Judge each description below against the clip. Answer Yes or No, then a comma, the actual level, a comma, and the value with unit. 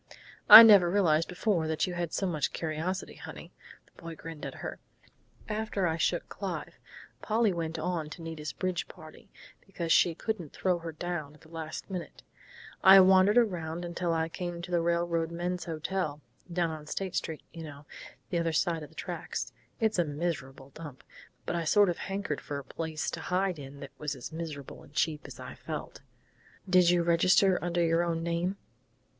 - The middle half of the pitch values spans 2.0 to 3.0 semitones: Yes, narrow, 2.4 semitones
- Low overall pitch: No, medium, 170 Hz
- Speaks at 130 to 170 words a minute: No, average, 185 wpm